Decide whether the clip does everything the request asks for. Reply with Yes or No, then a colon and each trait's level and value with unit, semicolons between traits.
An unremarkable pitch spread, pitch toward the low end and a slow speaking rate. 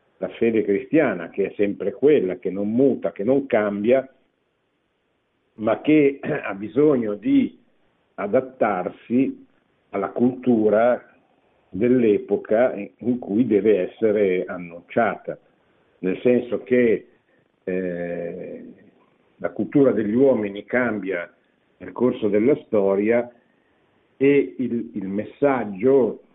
Yes: average, 4.7 semitones; low, 120 Hz; slow, 100 wpm